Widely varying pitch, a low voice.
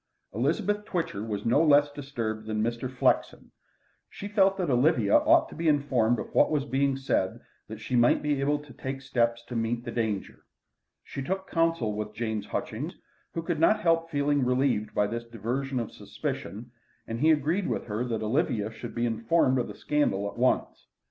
No: average, 4.6 semitones; low, 125 Hz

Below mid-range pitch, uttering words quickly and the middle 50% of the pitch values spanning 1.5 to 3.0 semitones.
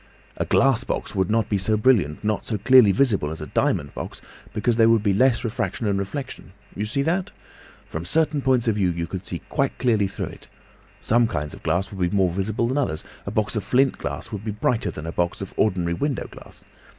No: low, 105 Hz; fast, 220 wpm; average, 4.8 semitones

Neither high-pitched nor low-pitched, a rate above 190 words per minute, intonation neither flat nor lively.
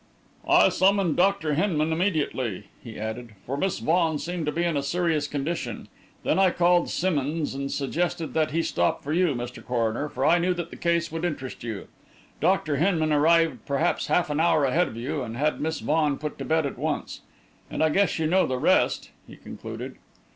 Yes: medium, 155 Hz; average, 200 wpm; average, 3.7 semitones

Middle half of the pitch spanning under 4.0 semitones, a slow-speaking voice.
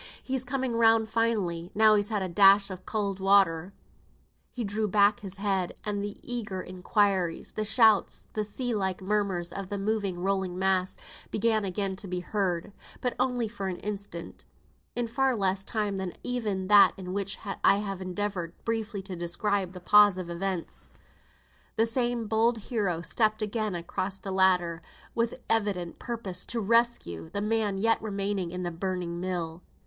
No: average, 2.8 semitones; average, 165 wpm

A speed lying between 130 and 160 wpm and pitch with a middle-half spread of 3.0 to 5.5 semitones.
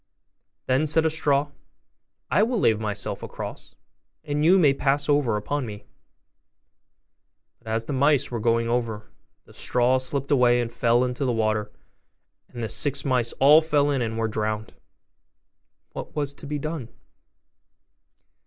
Yes: average, 155 wpm; average, 4.1 semitones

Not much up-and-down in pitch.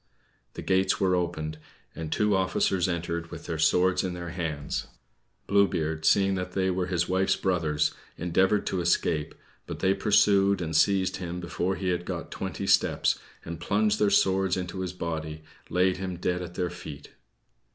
Yes: narrow, 2.2 semitones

